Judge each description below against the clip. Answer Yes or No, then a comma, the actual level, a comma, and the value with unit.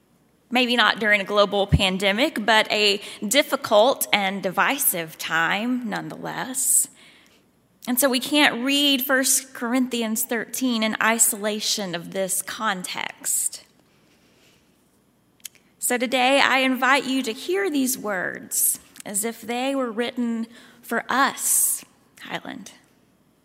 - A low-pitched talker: No, high, 235 Hz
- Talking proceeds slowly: Yes, slow, 110 wpm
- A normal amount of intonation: Yes, average, 3.8 semitones